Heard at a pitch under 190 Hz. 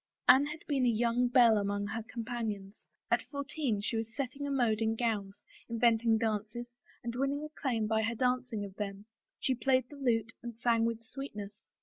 No: high, 230 Hz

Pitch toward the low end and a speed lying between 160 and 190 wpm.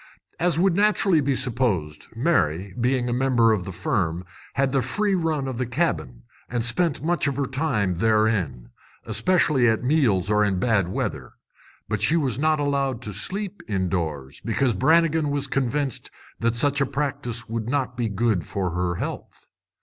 Yes: low, 125 Hz; average, 170 wpm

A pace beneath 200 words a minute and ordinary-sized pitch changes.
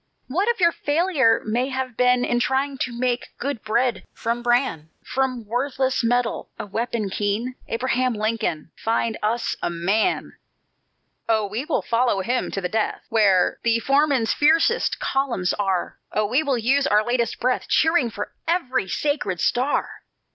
Yes: average, 155 wpm; average, 3.5 semitones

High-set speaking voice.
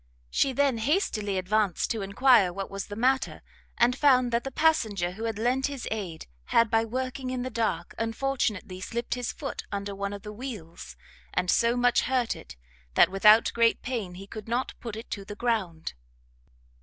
Yes: high, 225 Hz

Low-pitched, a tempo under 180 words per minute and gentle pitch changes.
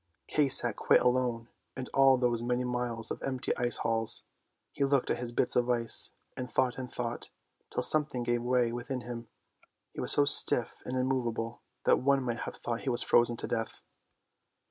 No: low, 125 Hz; average, 190 wpm; narrow, 1.5 semitones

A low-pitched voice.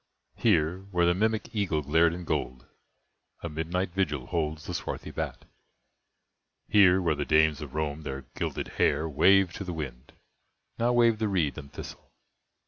Yes: very low, 80 Hz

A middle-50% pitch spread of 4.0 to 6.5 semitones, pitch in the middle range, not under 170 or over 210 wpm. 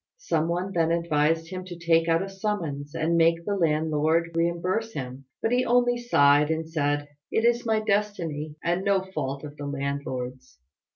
Yes: average, 4.4 semitones; medium, 165 Hz; average, 175 wpm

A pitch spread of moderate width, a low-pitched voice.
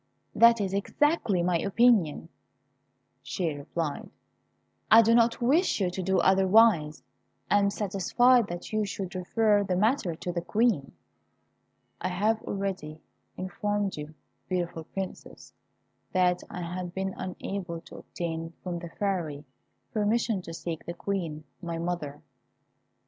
No: average, 3.4 semitones; medium, 185 Hz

